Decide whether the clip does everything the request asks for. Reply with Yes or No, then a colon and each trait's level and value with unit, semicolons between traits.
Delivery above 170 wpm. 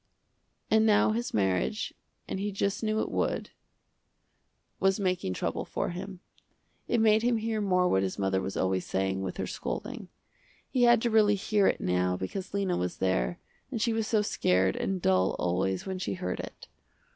Yes: average, 180 wpm